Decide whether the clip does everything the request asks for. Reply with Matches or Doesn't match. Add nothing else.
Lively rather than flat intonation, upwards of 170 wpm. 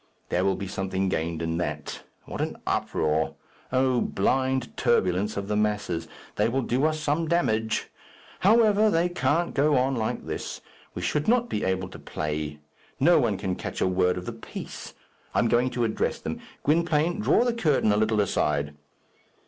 Matches